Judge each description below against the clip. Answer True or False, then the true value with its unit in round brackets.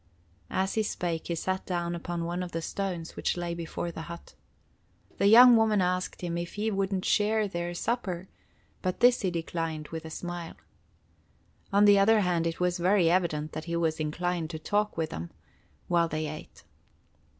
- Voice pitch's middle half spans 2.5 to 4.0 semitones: True (2.9 semitones)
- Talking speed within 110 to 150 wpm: False (185 wpm)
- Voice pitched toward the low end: False (175 Hz)